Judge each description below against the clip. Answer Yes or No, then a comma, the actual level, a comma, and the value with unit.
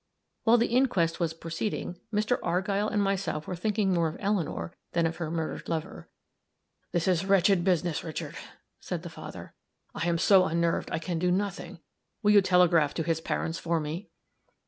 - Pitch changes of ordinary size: Yes, average, 3.1 semitones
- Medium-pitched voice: Yes, medium, 175 Hz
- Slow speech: No, average, 175 wpm